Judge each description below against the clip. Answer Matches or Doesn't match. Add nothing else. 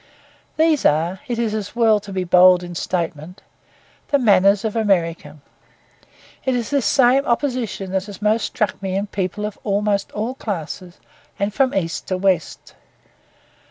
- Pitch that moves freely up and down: Doesn't match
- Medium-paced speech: Matches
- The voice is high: Matches